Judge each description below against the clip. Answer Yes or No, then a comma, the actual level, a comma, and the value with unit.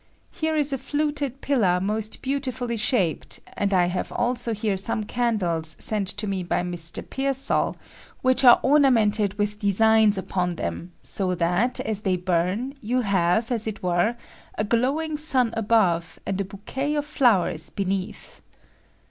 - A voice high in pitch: Yes, high, 215 Hz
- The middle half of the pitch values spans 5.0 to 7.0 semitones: Yes, average, 5.3 semitones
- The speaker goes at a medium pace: Yes, average, 150 wpm